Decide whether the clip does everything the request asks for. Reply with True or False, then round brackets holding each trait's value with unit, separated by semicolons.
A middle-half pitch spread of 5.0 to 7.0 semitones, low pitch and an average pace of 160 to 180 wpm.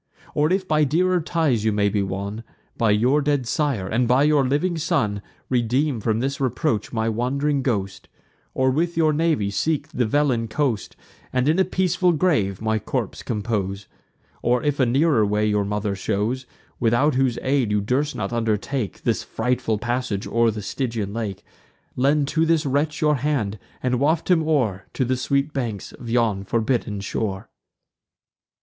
True (5.5 semitones; 125 Hz; 170 wpm)